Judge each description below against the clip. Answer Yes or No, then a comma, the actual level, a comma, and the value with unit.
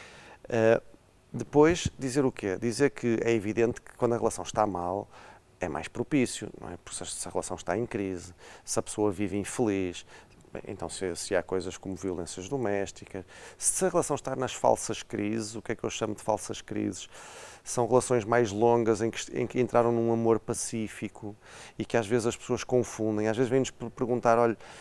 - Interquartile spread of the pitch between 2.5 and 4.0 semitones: Yes, average, 3.2 semitones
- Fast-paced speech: Yes, fast, 195 wpm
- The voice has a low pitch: Yes, low, 115 Hz